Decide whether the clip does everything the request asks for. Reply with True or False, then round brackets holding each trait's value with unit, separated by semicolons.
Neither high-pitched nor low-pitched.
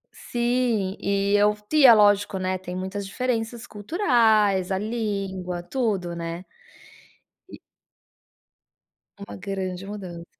False (200 Hz)